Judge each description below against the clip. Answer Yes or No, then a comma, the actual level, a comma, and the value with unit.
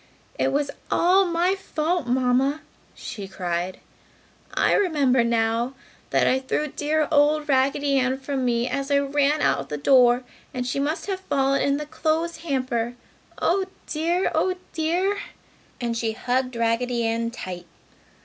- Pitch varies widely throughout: No, average, 4.3 semitones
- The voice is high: Yes, very high, 275 Hz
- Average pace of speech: Yes, average, 150 wpm